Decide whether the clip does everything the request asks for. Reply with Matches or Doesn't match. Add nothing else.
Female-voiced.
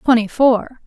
Matches